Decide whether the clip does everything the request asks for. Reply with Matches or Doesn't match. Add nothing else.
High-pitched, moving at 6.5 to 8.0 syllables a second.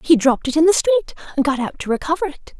Matches